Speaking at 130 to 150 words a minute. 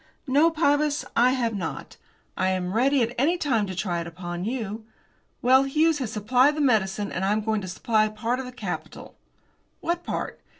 No: average, 195 wpm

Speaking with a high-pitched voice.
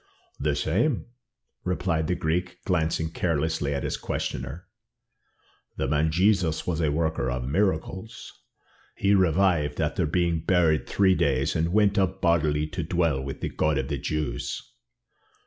No: very low, 80 Hz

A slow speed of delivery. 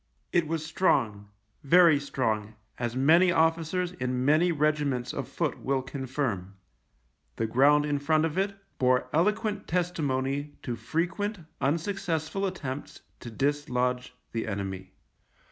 Yes: slow, 125 wpm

